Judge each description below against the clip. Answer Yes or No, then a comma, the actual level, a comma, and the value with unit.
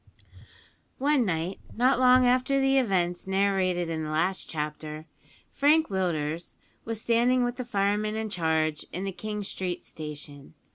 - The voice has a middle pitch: No, high, 195 Hz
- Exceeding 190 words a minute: No, average, 145 wpm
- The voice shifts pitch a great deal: Yes, wide, 7.0 semitones